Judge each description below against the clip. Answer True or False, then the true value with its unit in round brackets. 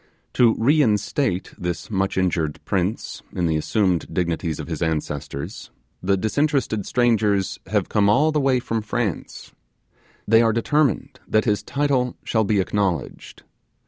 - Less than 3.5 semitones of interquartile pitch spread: False (5.1 semitones)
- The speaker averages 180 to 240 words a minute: False (140 wpm)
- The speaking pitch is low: True (105 Hz)